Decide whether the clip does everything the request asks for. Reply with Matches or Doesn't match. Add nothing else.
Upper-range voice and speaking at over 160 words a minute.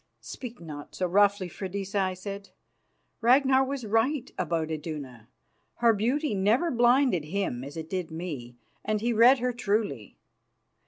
Doesn't match